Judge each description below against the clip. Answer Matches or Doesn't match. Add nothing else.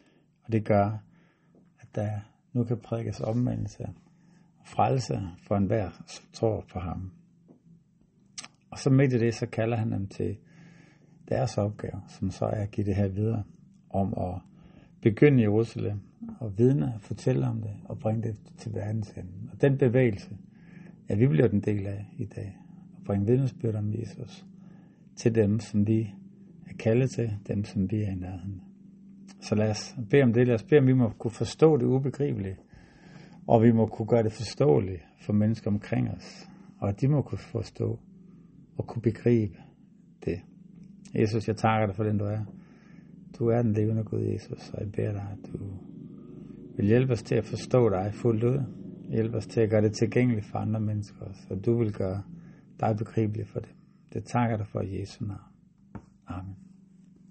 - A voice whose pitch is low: Matches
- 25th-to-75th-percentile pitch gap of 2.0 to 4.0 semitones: Doesn't match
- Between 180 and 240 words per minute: Matches